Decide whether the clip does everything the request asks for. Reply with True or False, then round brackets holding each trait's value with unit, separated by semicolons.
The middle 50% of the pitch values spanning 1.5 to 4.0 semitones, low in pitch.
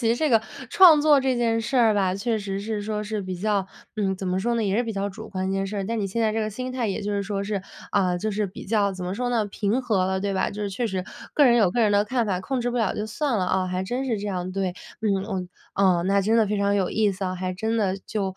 False (2.9 semitones; 205 Hz)